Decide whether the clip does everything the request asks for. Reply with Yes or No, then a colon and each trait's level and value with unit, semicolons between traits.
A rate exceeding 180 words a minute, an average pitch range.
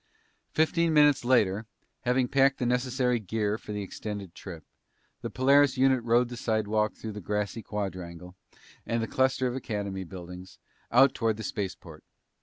No: average, 155 wpm; average, 4.3 semitones